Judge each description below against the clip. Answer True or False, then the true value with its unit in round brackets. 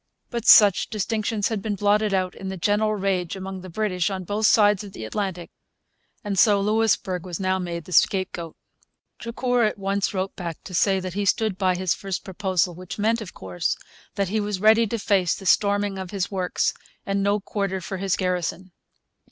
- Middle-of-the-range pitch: False (195 Hz)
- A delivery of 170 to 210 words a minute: True (195 wpm)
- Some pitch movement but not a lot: False (2.1 semitones)